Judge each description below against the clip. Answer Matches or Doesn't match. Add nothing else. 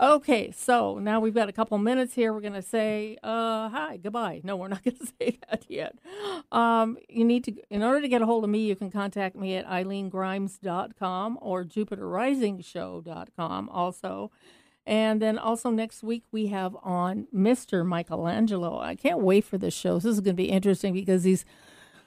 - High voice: Matches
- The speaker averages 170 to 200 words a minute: Matches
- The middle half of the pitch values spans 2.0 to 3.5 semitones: Matches